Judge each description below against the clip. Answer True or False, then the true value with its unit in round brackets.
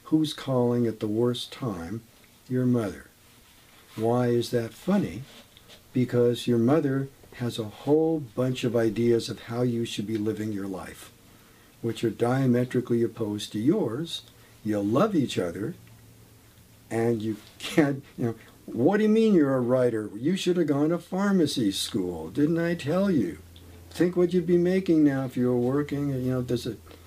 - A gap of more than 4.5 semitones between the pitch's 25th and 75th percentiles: False (4.2 semitones)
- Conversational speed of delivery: True (170 wpm)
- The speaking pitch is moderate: False (120 Hz)